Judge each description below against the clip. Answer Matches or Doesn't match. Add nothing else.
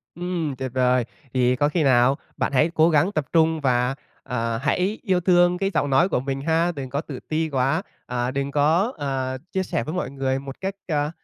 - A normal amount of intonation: Matches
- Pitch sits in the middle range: Matches